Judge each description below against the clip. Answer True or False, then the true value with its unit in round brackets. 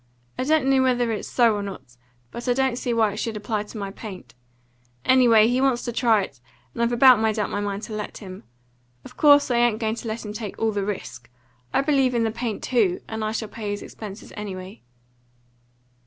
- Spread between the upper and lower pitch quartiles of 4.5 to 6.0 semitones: False (2.8 semitones)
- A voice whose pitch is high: True (225 Hz)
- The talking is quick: True (225 wpm)